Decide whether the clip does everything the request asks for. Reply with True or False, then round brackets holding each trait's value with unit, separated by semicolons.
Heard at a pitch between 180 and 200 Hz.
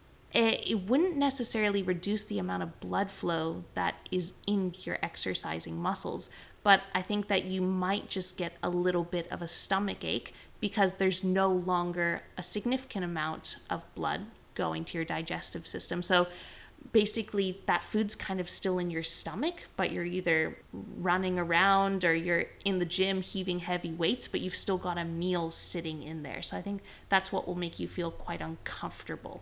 True (185 Hz)